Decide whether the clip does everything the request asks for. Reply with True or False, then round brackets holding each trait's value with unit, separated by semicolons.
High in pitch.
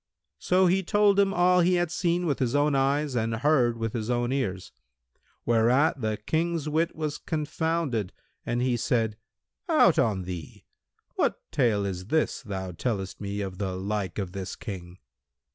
False (120 Hz)